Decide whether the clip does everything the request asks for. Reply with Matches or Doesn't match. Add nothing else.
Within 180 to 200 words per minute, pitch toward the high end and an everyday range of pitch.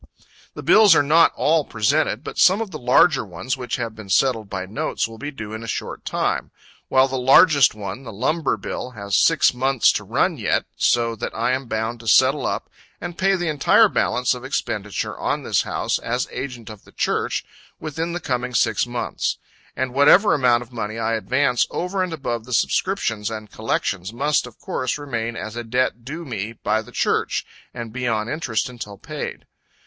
Doesn't match